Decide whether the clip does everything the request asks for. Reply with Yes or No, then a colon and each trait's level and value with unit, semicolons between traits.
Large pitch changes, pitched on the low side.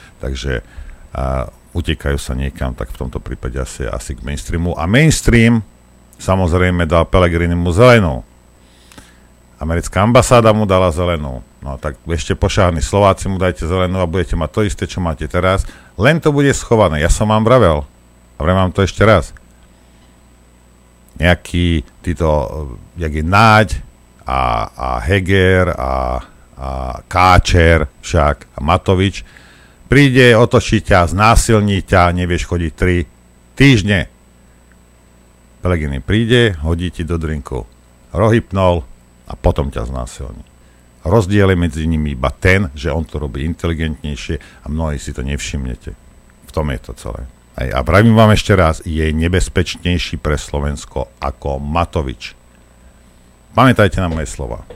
Yes: wide, 6.2 semitones; very low, 80 Hz